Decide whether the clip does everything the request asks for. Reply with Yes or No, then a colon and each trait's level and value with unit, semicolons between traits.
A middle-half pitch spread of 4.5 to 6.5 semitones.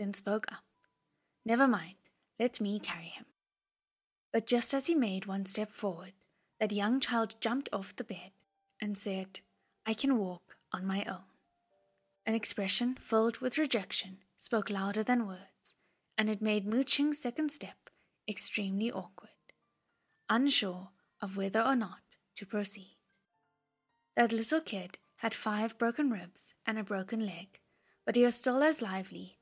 No: average, 3.9 semitones